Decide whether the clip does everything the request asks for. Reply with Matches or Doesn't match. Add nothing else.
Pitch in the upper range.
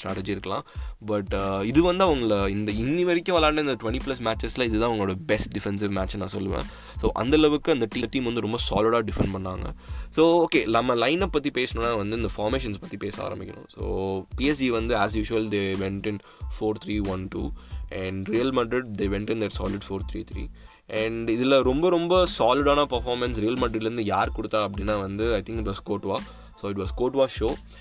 Doesn't match